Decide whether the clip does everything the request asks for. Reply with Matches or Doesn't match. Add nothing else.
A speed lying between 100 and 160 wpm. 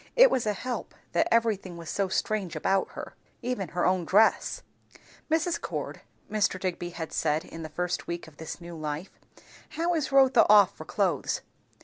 Doesn't match